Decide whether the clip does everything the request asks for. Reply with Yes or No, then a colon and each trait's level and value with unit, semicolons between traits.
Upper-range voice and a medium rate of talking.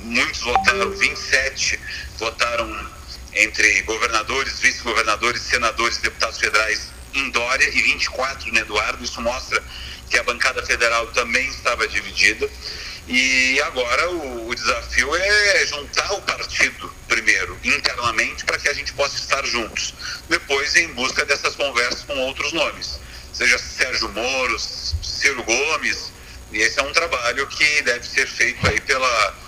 No: low, 115 Hz; average, 140 wpm